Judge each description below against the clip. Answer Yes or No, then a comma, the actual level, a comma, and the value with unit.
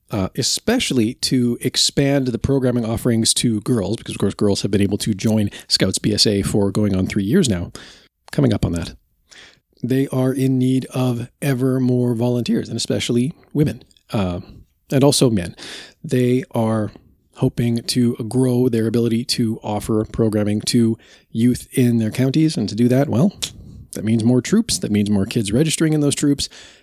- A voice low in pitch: Yes, low, 120 Hz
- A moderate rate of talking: Yes, average, 170 wpm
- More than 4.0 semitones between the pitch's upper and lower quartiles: No, average, 3.0 semitones